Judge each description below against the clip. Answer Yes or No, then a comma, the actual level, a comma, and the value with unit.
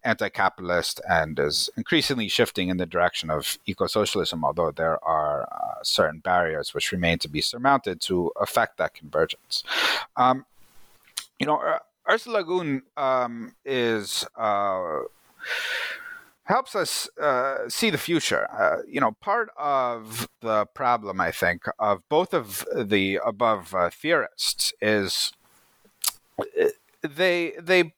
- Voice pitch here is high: No, low, 135 Hz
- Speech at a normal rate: No, slow, 130 wpm